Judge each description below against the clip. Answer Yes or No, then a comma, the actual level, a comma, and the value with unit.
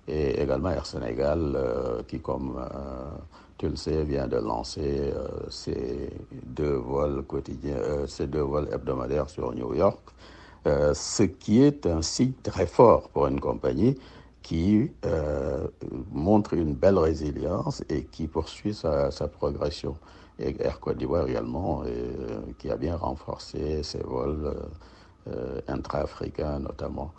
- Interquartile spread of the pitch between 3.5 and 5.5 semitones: Yes, average, 3.8 semitones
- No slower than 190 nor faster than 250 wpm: No, slow, 145 wpm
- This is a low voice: Yes, very low, 75 Hz